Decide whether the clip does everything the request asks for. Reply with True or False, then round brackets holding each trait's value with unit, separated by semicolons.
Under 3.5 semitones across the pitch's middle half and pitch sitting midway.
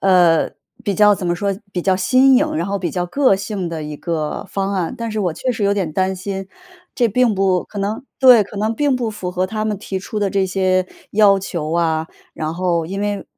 False (2.9 semitones; 195 Hz)